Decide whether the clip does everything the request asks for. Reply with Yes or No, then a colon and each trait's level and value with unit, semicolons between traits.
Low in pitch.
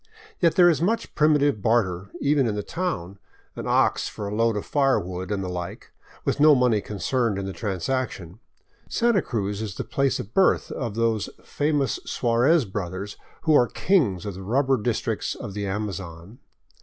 Yes: low, 110 Hz